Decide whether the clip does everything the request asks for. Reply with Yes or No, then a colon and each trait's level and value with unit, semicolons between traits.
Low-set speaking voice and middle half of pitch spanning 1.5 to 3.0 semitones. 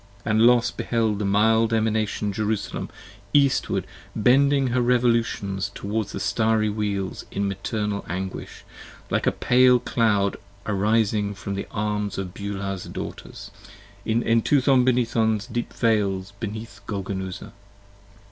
Yes: low, 110 Hz; narrow, 2.6 semitones